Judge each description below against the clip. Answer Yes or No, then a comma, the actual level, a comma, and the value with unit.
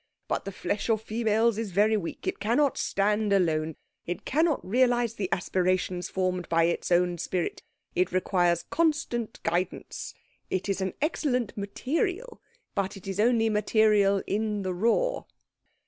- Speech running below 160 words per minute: Yes, average, 145 wpm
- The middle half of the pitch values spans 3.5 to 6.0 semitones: Yes, average, 4.1 semitones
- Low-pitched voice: No, high, 205 Hz